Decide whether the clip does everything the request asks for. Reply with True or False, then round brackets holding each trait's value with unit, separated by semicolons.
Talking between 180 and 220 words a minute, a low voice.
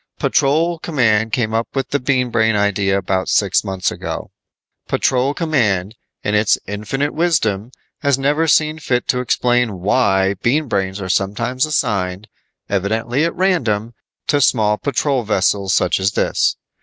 False (145 wpm; 115 Hz)